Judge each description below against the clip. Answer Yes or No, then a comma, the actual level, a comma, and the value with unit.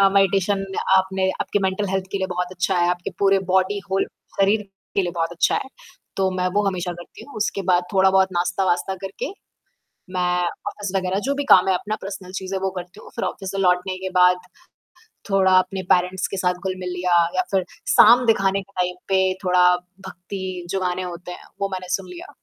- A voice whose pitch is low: No, high, 190 Hz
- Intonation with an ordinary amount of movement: No, narrow, 1.4 semitones